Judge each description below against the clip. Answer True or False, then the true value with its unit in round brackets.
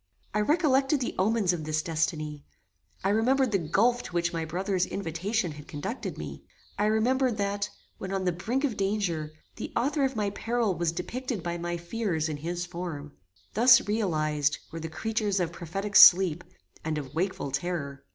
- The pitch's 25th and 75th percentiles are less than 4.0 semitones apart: False (5.3 semitones)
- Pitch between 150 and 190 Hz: True (185 Hz)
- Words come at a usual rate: True (175 wpm)